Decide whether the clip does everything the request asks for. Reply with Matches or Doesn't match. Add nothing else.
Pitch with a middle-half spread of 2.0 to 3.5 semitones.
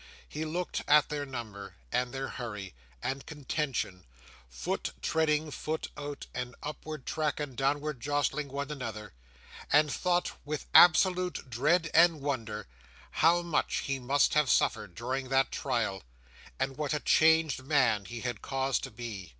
Doesn't match